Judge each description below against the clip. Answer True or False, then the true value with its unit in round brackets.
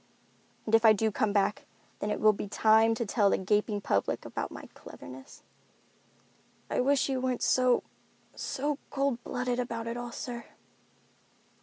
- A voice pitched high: True (230 Hz)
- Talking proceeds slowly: False (155 wpm)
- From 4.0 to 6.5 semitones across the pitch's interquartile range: False (3.0 semitones)